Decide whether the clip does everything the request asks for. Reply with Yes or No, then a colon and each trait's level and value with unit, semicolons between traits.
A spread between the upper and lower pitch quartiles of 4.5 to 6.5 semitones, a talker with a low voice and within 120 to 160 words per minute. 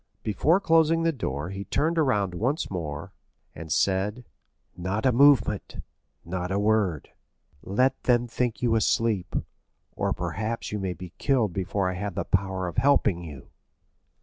Yes: wide, 5.5 semitones; low, 105 Hz; average, 150 wpm